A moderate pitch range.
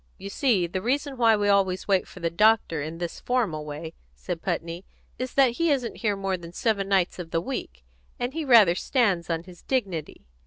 No: wide, 6.0 semitones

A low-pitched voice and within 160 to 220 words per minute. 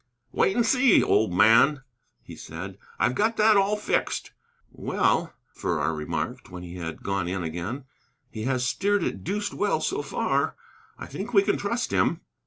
Yes: low, 130 Hz; average, 170 wpm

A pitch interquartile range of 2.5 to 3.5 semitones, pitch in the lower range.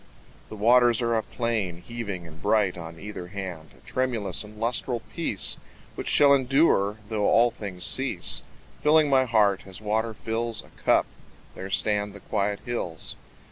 Yes: average, 3.2 semitones; low, 110 Hz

